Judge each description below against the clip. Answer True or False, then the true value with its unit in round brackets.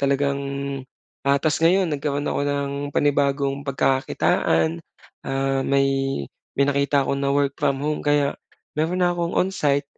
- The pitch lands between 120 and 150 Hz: True (140 Hz)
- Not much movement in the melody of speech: True (1.2 semitones)